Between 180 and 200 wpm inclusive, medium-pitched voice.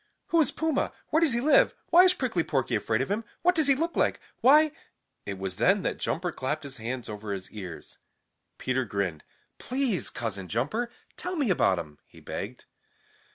Yes: average, 195 wpm; medium, 160 Hz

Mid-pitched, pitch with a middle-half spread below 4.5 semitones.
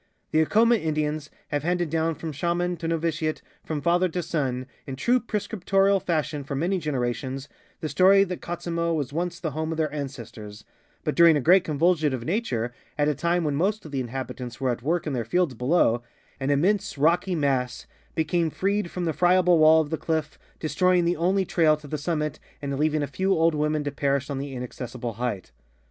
Yes: medium, 155 Hz; average, 3.9 semitones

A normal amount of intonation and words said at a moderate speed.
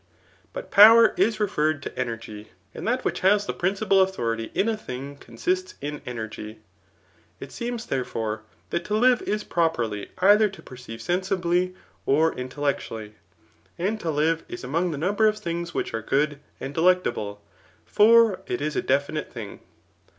No: wide, 7.9 semitones; average, 160 wpm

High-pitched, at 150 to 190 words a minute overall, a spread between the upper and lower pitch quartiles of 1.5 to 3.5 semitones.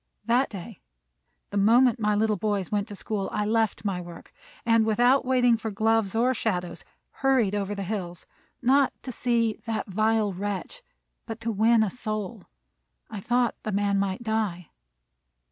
Yes: high, 215 Hz; average, 160 wpm; average, 2.7 semitones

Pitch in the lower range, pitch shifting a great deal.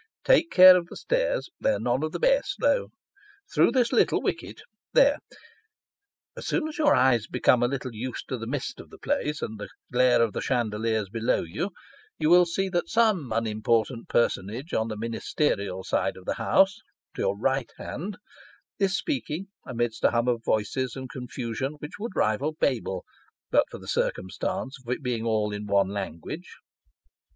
Yes: low, 125 Hz; wide, 8.4 semitones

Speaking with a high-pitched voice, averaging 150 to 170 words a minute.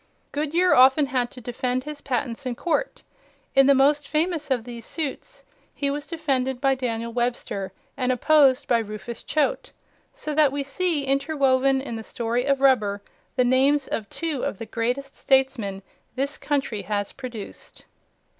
Yes: very high, 265 Hz; average, 160 wpm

